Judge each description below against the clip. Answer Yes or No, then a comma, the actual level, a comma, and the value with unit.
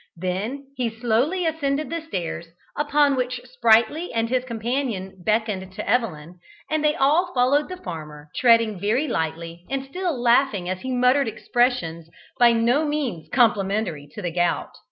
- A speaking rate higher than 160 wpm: No, average, 155 wpm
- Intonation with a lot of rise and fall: Yes, wide, 6.6 semitones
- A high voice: Yes, high, 235 Hz